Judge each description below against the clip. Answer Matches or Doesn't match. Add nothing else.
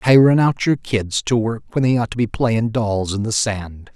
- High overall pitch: Doesn't match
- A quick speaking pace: Matches